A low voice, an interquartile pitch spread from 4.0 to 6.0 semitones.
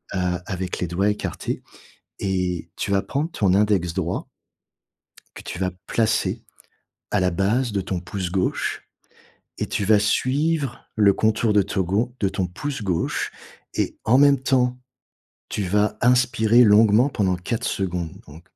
Yes: low, 105 Hz; average, 4.4 semitones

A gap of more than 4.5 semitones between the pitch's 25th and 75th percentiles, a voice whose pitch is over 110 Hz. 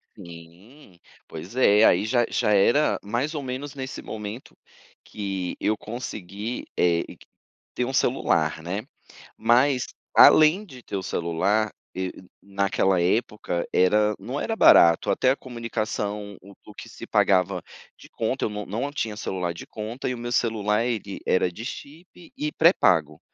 No: average, 4.9 semitones; low, 105 Hz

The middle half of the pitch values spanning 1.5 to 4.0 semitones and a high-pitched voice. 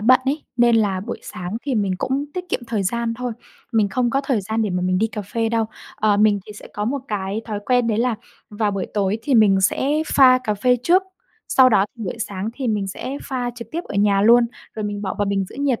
Yes: average, 3.5 semitones; high, 220 Hz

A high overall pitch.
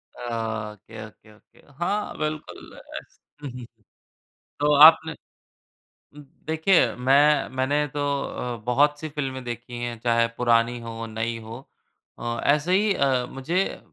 No: low, 130 Hz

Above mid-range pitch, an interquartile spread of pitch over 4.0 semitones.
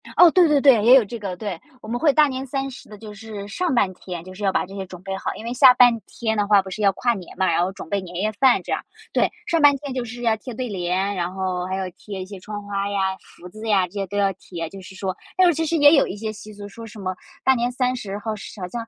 Yes: high, 210 Hz; average, 4.4 semitones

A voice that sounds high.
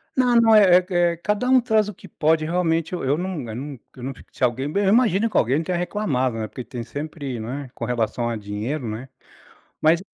No: medium, 155 Hz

